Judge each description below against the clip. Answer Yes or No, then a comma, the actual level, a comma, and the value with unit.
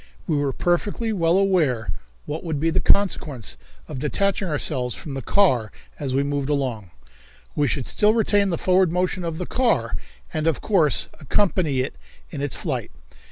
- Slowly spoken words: No, average, 170 wpm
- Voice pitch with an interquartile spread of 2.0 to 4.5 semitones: No, average, 5.2 semitones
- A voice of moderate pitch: Yes, medium, 155 Hz